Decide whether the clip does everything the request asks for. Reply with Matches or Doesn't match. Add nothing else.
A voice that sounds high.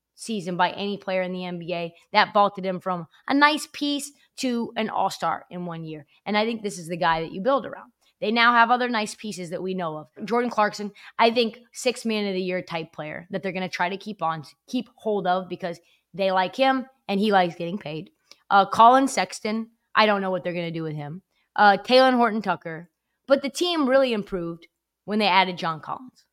Matches